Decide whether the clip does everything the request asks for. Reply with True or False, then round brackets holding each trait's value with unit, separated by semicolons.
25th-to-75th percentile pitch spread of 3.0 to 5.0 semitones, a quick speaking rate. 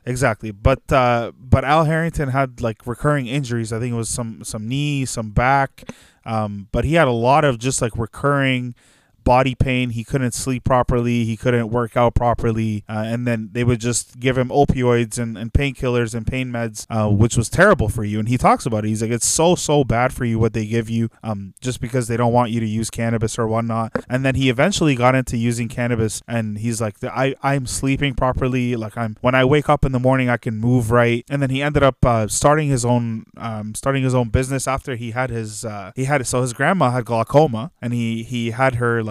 False (2.5 semitones; 230 wpm)